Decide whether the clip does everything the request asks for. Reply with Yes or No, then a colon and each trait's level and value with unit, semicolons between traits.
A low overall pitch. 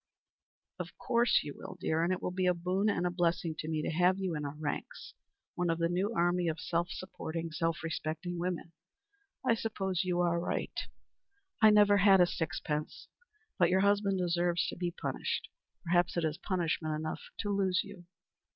No: medium, 175 Hz